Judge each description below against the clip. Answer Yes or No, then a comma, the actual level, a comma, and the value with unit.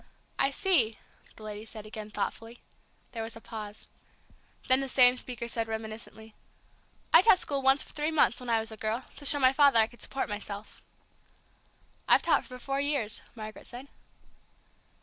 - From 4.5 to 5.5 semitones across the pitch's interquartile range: No, average, 3.7 semitones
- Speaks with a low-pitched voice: No, high, 235 Hz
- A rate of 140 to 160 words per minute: No, average, 175 wpm